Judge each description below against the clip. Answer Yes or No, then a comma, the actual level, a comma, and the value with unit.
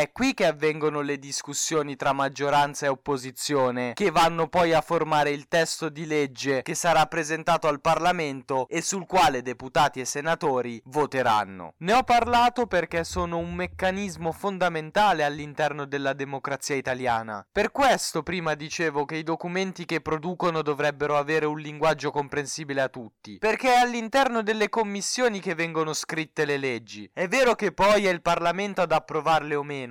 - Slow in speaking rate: No, average, 160 wpm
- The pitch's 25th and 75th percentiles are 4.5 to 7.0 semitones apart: No, average, 3.6 semitones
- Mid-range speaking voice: Yes, medium, 155 Hz